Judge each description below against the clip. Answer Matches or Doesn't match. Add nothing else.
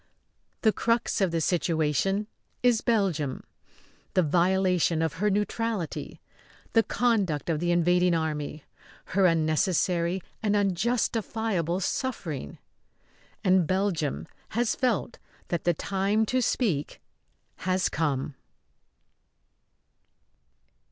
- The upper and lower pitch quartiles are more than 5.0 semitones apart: Doesn't match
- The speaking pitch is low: Doesn't match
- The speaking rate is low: Matches